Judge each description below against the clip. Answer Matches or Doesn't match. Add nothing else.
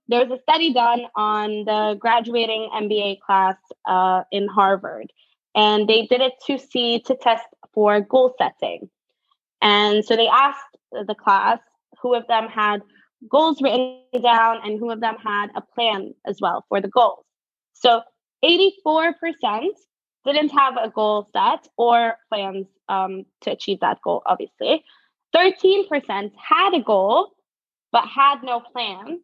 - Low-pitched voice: Doesn't match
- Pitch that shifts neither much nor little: Matches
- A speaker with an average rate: Matches